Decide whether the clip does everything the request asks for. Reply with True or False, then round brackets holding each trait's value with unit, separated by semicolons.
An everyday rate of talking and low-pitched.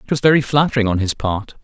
False (255 wpm; 120 Hz)